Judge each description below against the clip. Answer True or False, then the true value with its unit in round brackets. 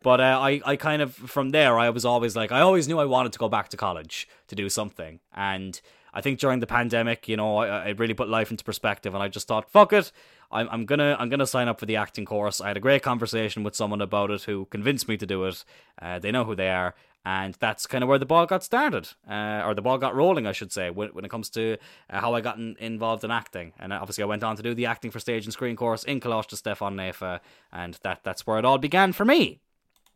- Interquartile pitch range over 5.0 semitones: False (3.7 semitones)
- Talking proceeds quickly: True (275 wpm)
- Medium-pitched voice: False (115 Hz)